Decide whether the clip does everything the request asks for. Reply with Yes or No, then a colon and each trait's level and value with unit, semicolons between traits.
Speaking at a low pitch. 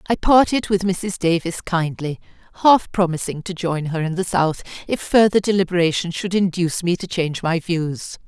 No: medium, 175 Hz